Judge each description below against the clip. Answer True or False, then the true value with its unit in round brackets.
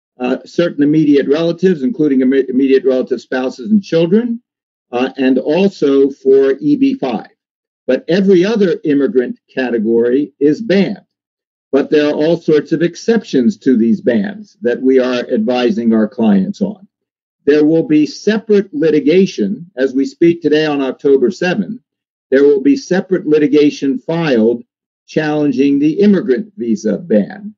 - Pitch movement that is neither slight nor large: False (7.0 semitones)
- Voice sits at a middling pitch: True (155 Hz)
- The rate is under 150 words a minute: True (135 wpm)